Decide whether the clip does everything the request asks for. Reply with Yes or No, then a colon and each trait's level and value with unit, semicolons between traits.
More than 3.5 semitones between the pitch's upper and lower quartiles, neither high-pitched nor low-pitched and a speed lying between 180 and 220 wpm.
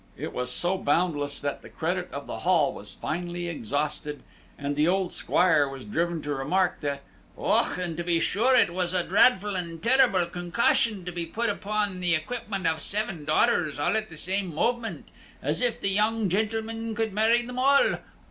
Yes: average, 5.1 semitones; medium, 180 Hz; average, 185 wpm